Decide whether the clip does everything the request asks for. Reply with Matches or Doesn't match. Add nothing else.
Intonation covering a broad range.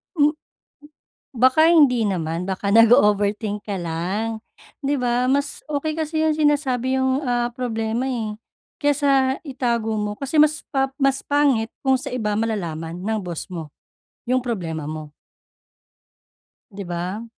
Doesn't match